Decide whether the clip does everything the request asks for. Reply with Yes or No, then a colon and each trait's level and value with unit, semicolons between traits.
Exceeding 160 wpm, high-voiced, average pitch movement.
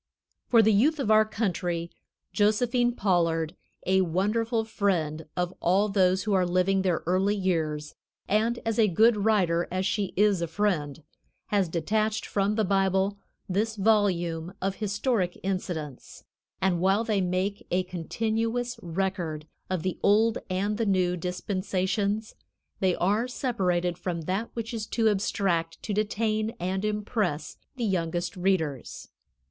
No: average, 140 wpm; high, 195 Hz; average, 3.2 semitones